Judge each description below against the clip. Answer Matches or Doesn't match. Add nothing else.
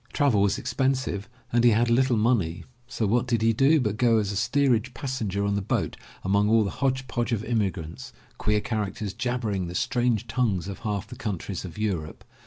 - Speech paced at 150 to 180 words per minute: Doesn't match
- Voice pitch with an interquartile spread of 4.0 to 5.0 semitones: Doesn't match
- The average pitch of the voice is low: Matches